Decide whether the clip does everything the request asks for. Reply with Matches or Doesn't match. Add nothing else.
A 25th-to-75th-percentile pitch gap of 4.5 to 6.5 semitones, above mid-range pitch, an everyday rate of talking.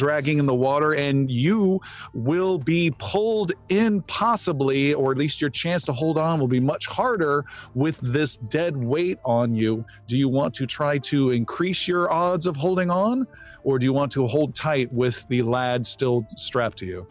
Doesn't match